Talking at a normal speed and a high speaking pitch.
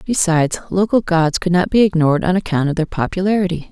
No: average, 195 wpm; medium, 180 Hz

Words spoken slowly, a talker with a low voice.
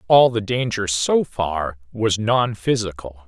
Yes: slow, 130 wpm; low, 105 Hz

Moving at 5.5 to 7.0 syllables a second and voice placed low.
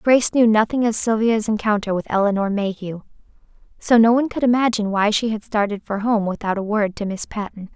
No: 5.9 syllables/s; high, 215 Hz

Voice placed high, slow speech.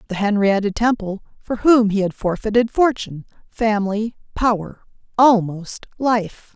Yes: high, 215 Hz; slow, 120 wpm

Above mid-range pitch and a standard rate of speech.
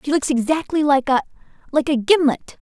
Yes: very high, 280 Hz; average, 155 wpm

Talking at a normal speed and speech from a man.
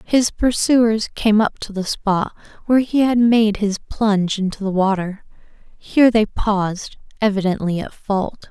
No: average, 155 wpm; female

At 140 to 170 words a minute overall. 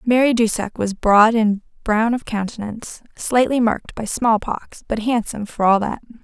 Yes: average, 165 wpm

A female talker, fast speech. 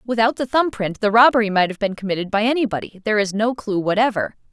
Yes: female; fast, 225 wpm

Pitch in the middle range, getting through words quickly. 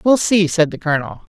Yes: medium, 180 Hz; fast, 220 wpm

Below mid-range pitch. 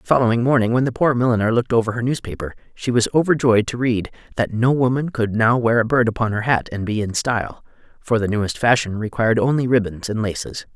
Yes: low, 115 Hz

